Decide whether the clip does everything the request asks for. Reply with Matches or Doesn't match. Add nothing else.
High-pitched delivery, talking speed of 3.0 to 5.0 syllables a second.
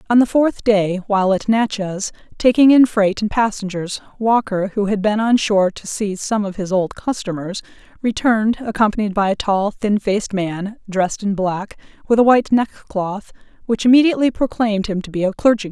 Doesn't match